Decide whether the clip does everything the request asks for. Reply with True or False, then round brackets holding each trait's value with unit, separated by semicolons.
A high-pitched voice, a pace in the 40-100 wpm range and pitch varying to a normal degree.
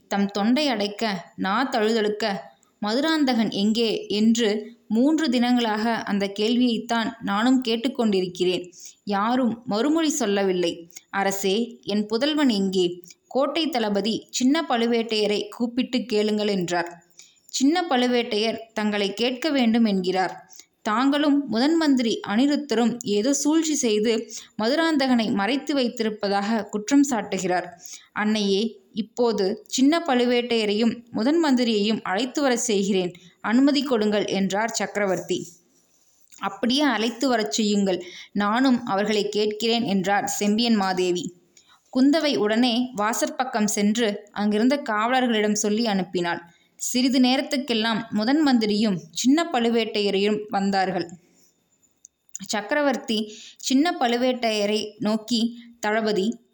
True (220 Hz; 95 wpm; 3.6 semitones)